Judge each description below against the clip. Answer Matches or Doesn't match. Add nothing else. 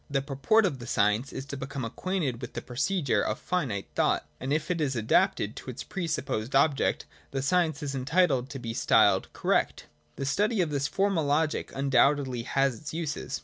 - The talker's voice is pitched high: Doesn't match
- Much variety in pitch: Doesn't match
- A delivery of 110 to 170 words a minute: Doesn't match